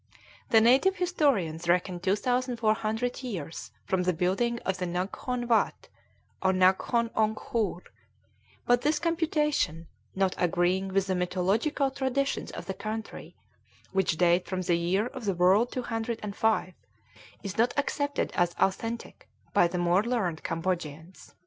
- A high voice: Yes, high, 200 Hz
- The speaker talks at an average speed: No, slow, 130 wpm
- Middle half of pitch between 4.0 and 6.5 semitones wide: Yes, average, 5.1 semitones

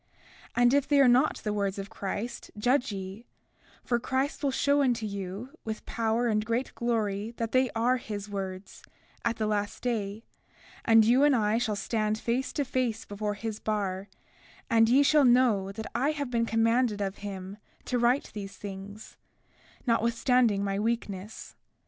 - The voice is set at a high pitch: Yes, high, 225 Hz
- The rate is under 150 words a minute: No, average, 165 wpm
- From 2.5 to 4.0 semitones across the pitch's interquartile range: Yes, average, 3.2 semitones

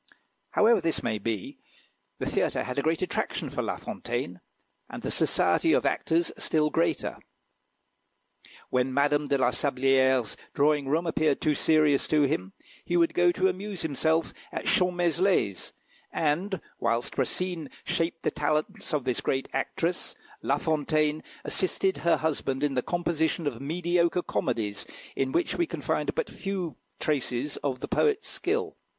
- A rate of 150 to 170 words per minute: Yes, average, 155 wpm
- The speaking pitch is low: No, medium, 155 Hz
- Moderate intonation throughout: Yes, average, 4.3 semitones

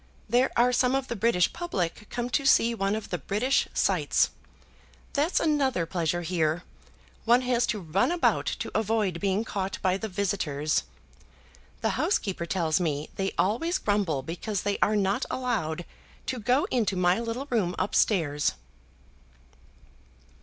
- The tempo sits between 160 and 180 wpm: No, average, 150 wpm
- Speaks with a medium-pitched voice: No, high, 200 Hz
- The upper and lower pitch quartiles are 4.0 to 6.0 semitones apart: Yes, wide, 5.4 semitones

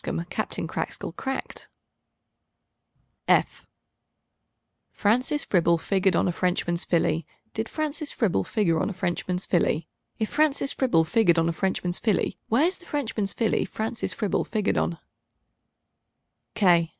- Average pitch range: No, wide, 5.8 semitones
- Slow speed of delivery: Yes, slow, 125 wpm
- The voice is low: No, high, 200 Hz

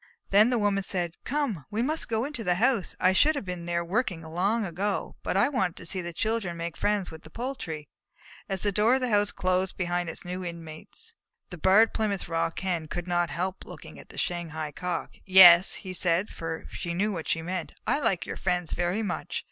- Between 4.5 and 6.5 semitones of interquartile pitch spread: No, average, 3.6 semitones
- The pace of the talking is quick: Yes, fast, 215 wpm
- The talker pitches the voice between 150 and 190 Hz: Yes, medium, 185 Hz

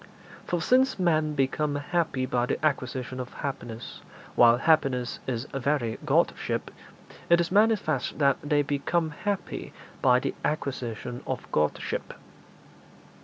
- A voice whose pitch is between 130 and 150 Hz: Yes, medium, 140 Hz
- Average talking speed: No, slow, 120 wpm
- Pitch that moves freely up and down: No, average, 4.1 semitones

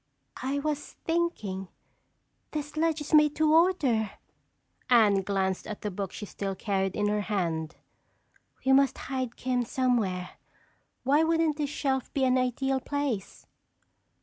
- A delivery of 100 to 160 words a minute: Yes, slow, 135 wpm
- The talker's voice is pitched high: Yes, very high, 255 Hz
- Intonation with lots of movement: Yes, wide, 6.4 semitones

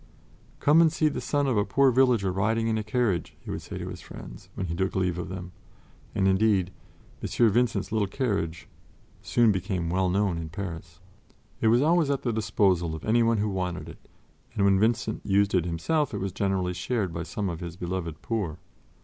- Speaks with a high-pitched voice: No, low, 100 Hz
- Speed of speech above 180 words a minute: Yes, average, 200 wpm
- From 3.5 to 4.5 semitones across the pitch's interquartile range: Yes, average, 4.2 semitones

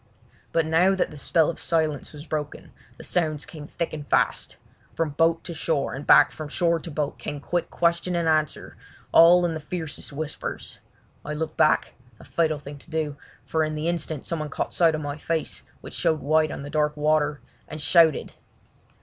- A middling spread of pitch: No, narrow, 1.9 semitones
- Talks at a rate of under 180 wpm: No, average, 190 wpm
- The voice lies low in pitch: No, medium, 155 Hz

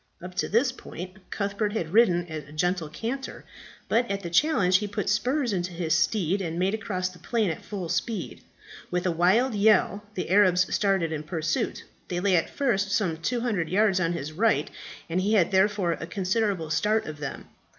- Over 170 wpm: Yes, average, 190 wpm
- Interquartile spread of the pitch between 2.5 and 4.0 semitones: Yes, average, 3.7 semitones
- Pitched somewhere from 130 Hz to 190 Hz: Yes, medium, 185 Hz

